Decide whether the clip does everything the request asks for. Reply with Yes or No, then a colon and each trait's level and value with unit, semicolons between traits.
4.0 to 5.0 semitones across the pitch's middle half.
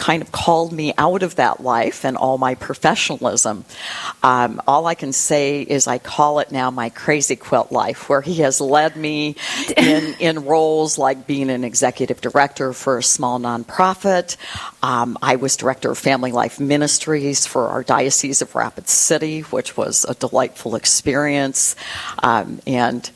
No: average, 2.9 semitones